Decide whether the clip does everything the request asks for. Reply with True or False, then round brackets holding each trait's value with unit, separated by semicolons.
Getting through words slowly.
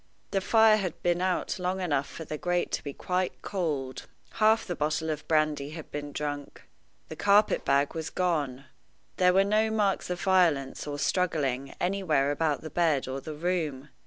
False (180 wpm)